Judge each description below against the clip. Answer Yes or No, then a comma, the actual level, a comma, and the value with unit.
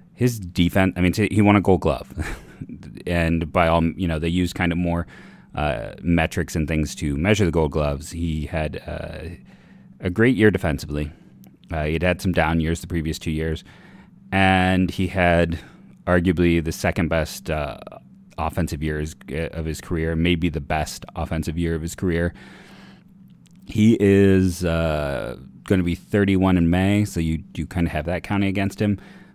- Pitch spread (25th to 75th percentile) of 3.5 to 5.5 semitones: No, average, 3.0 semitones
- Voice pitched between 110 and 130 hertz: No, very low, 85 Hz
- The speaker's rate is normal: Yes, average, 175 wpm